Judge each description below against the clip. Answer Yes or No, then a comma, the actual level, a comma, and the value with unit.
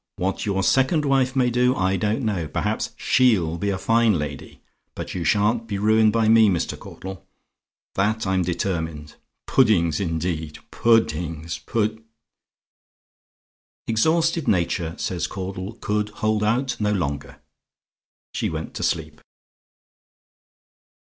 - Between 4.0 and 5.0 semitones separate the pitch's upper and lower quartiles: Yes, average, 4.5 semitones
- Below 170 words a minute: Yes, slow, 135 wpm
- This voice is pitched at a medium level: No, low, 105 Hz